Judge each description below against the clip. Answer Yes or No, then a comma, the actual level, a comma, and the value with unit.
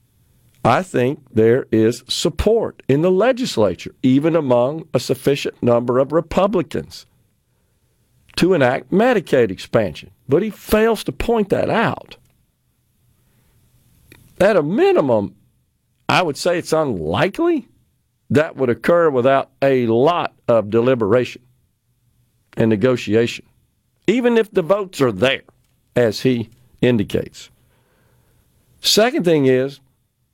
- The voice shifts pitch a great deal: Yes, wide, 6.4 semitones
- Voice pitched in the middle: No, low, 130 Hz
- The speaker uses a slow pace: Yes, slow, 110 wpm